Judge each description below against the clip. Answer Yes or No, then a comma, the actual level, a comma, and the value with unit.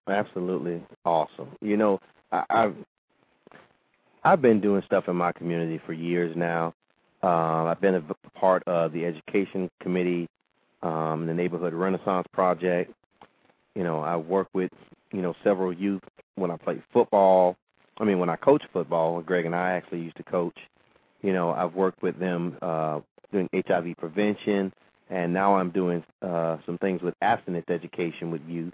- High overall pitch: No, very low, 90 Hz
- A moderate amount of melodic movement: No, narrow, 1.9 semitones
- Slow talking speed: No, average, 165 wpm